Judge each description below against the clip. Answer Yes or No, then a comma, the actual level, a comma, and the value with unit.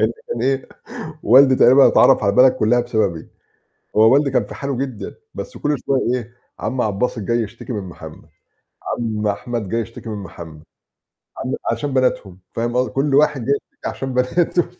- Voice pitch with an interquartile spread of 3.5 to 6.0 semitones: Yes, average, 3.8 semitones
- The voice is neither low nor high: No, low, 120 Hz